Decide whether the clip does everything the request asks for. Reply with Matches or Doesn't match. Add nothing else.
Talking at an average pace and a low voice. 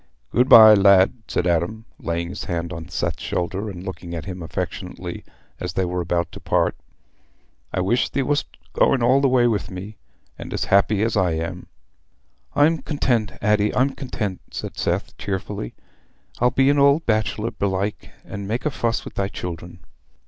Matches